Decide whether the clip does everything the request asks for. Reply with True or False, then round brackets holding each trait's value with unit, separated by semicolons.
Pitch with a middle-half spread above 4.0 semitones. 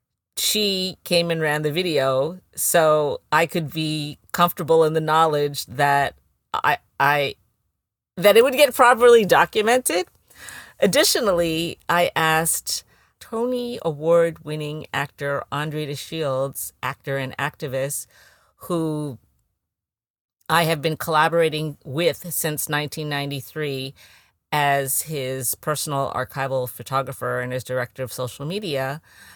False (3.7 semitones)